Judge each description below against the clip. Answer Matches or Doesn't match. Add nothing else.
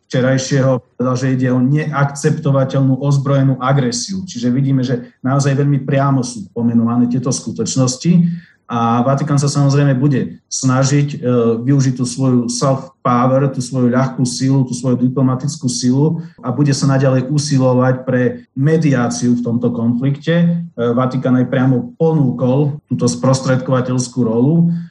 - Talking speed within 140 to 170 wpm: Doesn't match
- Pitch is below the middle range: Matches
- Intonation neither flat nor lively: Doesn't match